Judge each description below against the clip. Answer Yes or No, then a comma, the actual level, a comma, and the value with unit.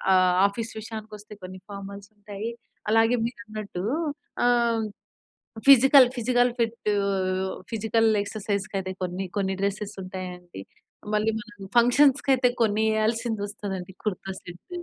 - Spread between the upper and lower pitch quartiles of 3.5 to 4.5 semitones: No, average, 2.9 semitones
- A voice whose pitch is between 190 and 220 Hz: Yes, high, 215 Hz